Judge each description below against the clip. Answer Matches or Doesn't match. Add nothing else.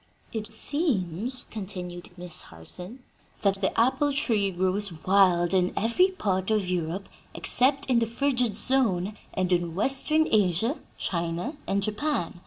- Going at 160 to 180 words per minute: Doesn't match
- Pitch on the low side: Doesn't match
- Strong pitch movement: Matches